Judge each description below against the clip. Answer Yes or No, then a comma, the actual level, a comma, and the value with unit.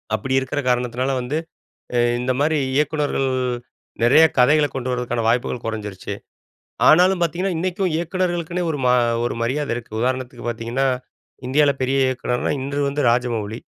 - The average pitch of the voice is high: No, low, 130 Hz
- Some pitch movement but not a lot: Yes, average, 4.1 semitones